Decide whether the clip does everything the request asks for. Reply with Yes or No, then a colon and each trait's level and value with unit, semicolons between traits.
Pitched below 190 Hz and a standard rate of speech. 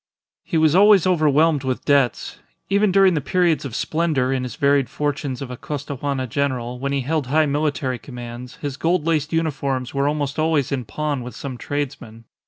Yes: medium, 140 Hz; average, 185 wpm